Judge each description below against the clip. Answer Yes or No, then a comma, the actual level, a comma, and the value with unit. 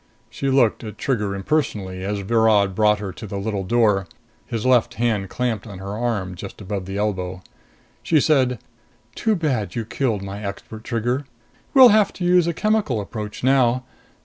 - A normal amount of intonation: Yes, average, 4.5 semitones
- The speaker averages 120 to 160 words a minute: No, average, 175 wpm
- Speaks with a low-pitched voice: Yes, low, 110 Hz